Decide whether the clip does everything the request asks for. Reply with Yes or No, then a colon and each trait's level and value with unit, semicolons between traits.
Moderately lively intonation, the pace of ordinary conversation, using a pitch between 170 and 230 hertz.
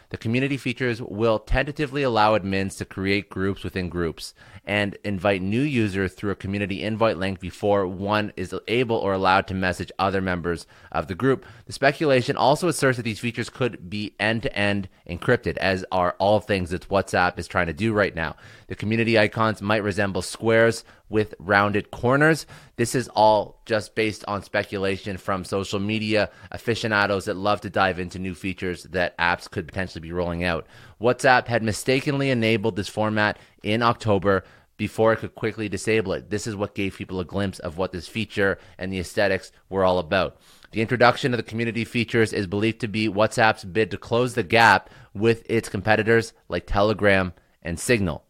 No: average, 3.1 semitones; average, 185 wpm; low, 105 Hz